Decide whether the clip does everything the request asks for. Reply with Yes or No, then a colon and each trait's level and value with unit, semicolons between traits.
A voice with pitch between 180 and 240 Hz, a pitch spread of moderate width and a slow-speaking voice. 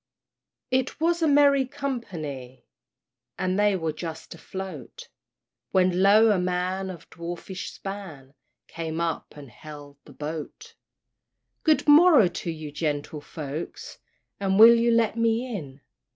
No: medium, 185 Hz; wide, 6.7 semitones; slow, 130 wpm